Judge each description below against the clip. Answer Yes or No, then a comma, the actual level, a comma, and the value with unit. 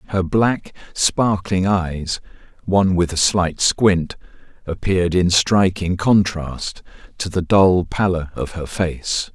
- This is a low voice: Yes, very low, 90 Hz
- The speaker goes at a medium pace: No, slow, 130 wpm